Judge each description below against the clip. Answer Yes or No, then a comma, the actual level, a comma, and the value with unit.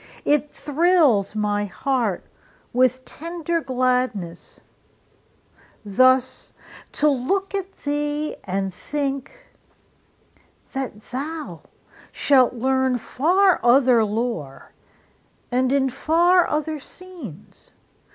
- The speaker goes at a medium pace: No, slow, 85 wpm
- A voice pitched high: Yes, very high, 265 Hz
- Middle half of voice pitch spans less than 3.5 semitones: No, average, 4.2 semitones